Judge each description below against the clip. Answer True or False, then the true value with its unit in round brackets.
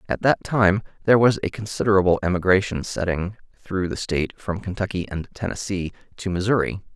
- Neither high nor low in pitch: False (95 Hz)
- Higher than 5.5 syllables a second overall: True (5.8 syllables/s)